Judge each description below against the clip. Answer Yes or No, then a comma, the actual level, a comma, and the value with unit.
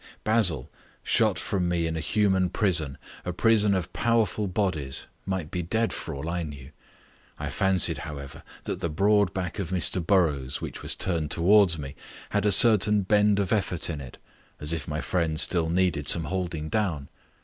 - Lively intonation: No, average, 4.2 semitones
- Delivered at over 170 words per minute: Yes, average, 180 wpm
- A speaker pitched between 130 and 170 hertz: No, very low, 90 Hz